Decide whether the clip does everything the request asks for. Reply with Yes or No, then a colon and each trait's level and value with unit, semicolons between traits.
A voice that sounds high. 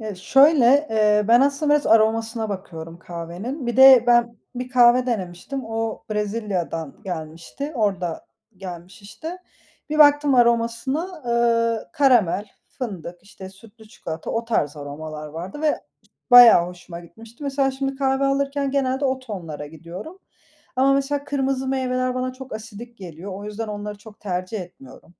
Yes: high, 230 Hz